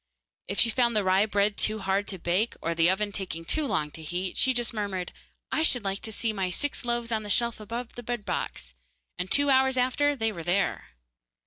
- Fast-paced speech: Yes, fast, 225 wpm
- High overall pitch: Yes, high, 210 Hz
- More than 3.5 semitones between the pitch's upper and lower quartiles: Yes, average, 4.2 semitones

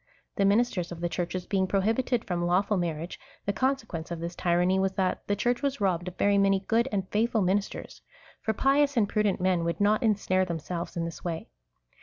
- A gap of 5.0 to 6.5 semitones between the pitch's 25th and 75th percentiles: No, average, 3.4 semitones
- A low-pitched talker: No, high, 190 Hz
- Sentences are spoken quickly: Yes, fast, 210 wpm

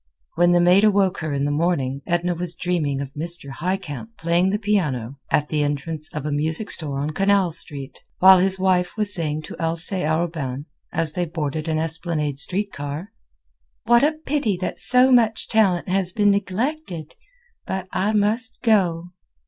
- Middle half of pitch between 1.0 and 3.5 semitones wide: No, average, 4.6 semitones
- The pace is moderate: Yes, average, 175 wpm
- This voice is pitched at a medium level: Yes, medium, 175 Hz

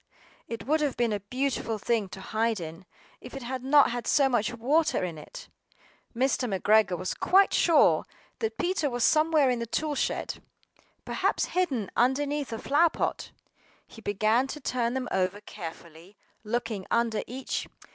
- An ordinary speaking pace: Yes, average, 160 wpm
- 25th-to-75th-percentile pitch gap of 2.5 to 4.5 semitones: No, average, 4.9 semitones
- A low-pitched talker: No, high, 240 Hz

